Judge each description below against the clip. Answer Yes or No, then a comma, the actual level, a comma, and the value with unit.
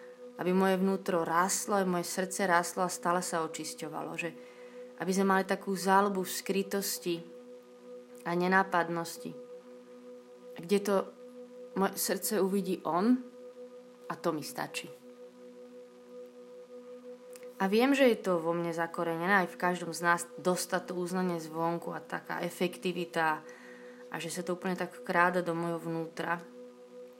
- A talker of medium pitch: Yes, medium, 180 Hz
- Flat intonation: No, average, 3.6 semitones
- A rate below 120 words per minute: No, average, 130 wpm